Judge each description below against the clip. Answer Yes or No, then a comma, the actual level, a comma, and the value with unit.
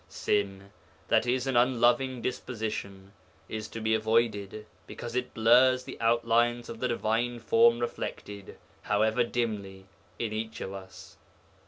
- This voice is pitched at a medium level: No, low, 115 Hz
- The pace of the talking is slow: Yes, slow, 130 wpm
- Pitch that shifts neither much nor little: No, narrow, 2.1 semitones